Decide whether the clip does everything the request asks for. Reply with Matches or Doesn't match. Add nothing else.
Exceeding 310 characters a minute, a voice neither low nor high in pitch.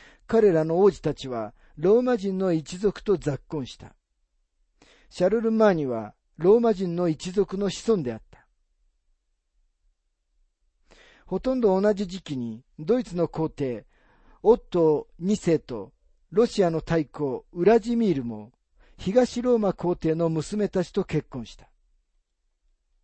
Doesn't match